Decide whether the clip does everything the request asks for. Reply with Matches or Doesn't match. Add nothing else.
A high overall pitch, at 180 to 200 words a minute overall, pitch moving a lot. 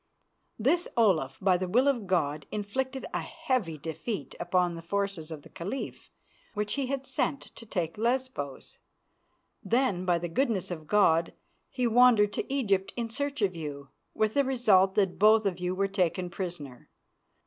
Doesn't match